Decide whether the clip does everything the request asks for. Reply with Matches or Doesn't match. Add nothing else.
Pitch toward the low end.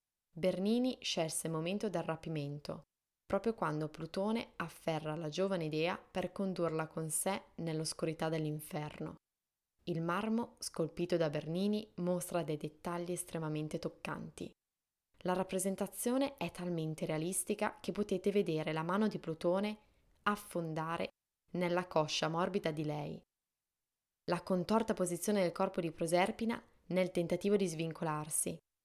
Doesn't match